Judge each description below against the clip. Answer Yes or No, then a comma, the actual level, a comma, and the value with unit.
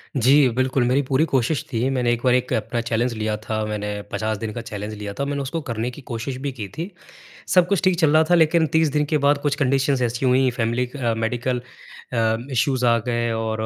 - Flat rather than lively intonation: No, average, 3.6 semitones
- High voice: No, low, 125 Hz